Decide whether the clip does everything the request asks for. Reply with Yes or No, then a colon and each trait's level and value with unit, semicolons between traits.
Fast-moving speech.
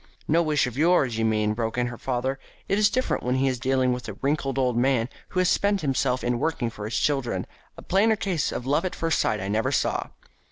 Yes: fast, 235 wpm